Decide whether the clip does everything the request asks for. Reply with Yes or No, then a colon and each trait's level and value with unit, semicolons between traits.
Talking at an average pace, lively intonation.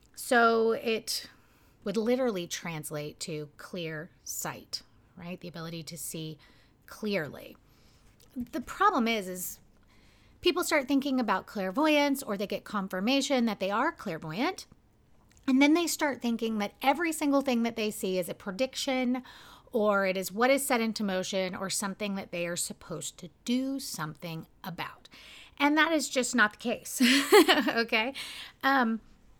Yes: average, 150 wpm; wide, 6.6 semitones